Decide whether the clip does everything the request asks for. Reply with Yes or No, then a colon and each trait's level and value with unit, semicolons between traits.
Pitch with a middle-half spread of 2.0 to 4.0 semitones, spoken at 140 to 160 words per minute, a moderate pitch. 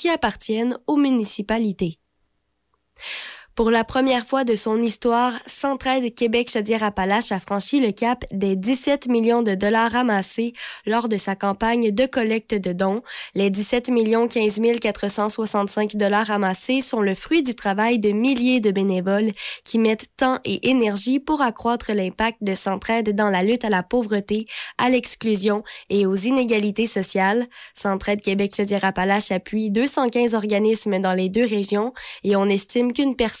No: average, 3.2 semitones; slow, 145 wpm; high, 220 Hz